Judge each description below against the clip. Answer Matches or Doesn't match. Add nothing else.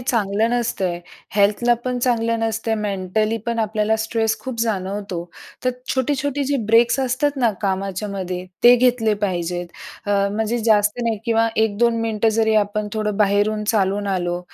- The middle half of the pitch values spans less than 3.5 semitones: Matches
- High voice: Matches